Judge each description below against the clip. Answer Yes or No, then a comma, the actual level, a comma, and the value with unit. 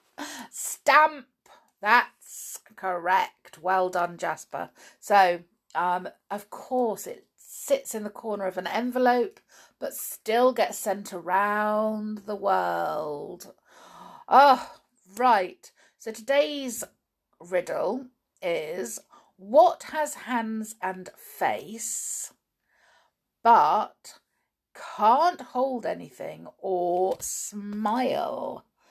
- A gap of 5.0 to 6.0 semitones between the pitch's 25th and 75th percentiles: Yes, wide, 5.6 semitones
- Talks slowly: Yes, slow, 85 wpm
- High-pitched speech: Yes, high, 220 Hz